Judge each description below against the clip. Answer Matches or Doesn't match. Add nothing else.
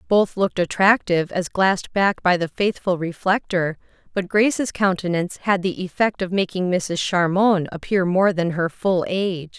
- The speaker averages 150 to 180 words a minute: Matches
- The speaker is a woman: Matches